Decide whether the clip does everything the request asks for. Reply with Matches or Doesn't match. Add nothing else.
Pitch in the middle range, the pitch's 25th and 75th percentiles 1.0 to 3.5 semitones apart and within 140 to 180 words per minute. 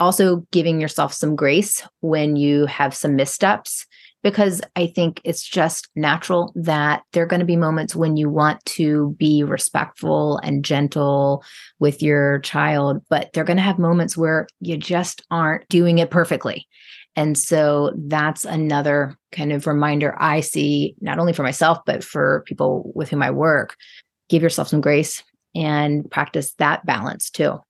Matches